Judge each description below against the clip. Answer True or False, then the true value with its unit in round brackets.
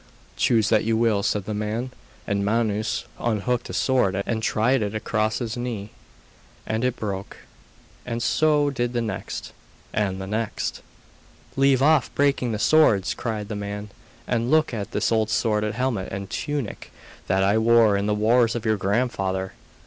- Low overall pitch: True (110 Hz)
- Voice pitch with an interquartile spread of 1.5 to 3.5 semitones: True (2.8 semitones)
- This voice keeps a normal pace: True (170 wpm)